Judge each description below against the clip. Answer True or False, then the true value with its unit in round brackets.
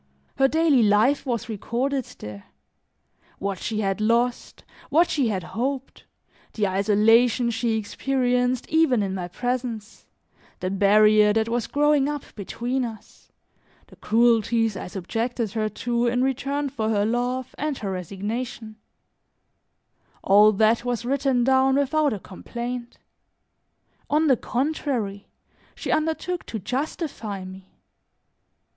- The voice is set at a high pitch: True (235 Hz)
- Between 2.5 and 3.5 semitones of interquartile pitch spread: False (3.9 semitones)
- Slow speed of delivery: True (125 wpm)